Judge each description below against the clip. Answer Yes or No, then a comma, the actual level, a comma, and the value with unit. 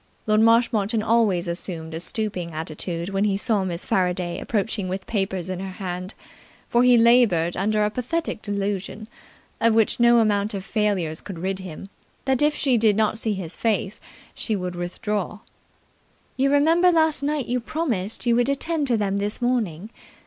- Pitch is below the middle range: No, high, 210 Hz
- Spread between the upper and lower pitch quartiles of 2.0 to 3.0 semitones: No, average, 4.2 semitones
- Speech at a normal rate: Yes, average, 170 wpm